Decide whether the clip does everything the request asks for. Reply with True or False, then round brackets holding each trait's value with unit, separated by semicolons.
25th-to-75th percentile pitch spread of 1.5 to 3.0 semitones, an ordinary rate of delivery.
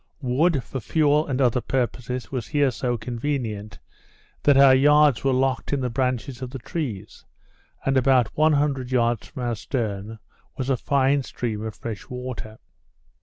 True (2.7 semitones; 155 wpm)